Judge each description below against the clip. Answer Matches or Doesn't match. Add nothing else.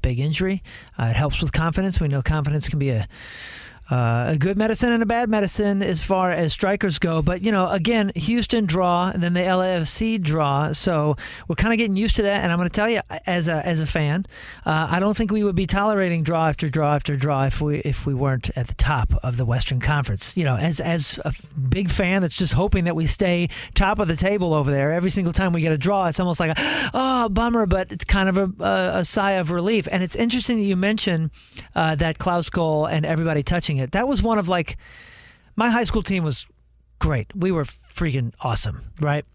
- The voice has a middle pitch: Matches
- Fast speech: Matches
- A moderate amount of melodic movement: Matches